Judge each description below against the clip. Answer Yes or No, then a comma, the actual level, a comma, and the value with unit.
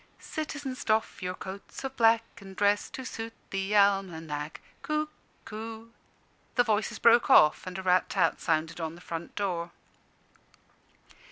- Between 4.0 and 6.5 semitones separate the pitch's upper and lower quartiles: Yes, average, 4.5 semitones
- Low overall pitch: No, high, 200 Hz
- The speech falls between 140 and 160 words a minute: Yes, average, 145 wpm